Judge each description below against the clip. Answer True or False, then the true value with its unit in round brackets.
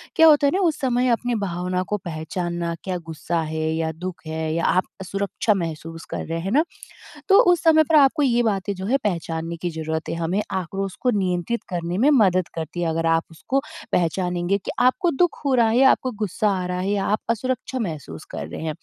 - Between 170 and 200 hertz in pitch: True (185 Hz)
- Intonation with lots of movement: True (6.5 semitones)